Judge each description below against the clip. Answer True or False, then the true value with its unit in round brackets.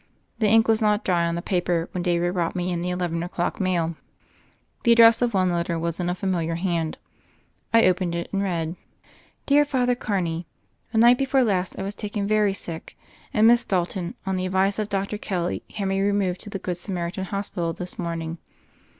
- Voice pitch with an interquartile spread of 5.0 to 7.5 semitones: False (3.2 semitones)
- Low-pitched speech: False (185 Hz)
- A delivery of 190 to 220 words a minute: True (200 wpm)